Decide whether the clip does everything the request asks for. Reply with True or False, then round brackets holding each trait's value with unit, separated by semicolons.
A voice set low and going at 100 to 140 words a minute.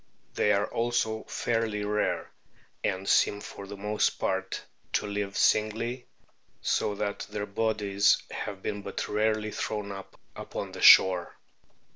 True (105 Hz; 135 wpm)